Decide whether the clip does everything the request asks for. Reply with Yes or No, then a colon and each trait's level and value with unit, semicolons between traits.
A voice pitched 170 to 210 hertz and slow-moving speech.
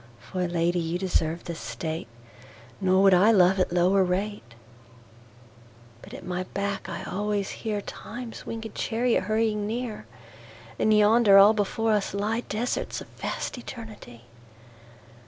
Yes: medium, 185 Hz; slow, 120 wpm